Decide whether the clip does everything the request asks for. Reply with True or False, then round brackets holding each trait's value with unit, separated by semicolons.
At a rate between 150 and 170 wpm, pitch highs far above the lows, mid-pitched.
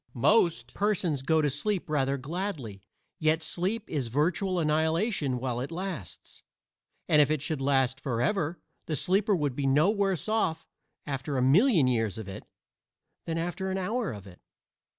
True (160 wpm; 5.8 semitones; 155 Hz)